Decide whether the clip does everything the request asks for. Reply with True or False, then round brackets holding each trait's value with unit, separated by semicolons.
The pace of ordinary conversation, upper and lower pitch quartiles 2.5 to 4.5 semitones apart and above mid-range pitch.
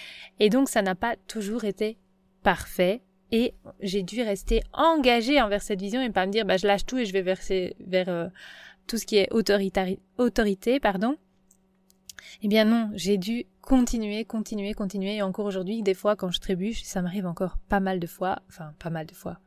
True (205 wpm; 3.0 semitones; 205 Hz)